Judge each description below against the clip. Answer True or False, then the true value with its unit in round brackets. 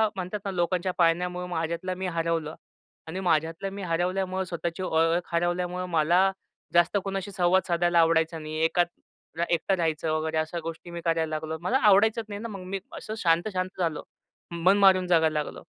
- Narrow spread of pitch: True (2.1 semitones)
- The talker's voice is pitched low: False (175 Hz)